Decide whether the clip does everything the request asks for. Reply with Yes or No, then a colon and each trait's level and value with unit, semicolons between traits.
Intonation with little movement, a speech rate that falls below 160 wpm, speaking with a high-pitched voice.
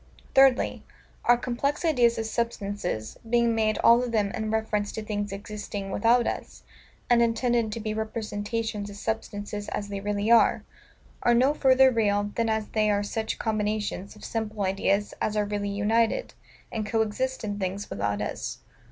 No: narrow, 2.2 semitones; average, 170 wpm; high, 215 Hz